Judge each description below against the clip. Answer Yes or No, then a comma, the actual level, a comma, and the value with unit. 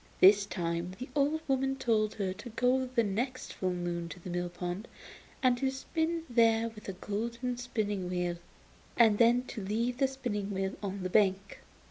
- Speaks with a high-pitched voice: Yes, high, 215 Hz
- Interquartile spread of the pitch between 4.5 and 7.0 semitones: Yes, average, 4.8 semitones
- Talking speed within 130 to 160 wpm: No, average, 180 wpm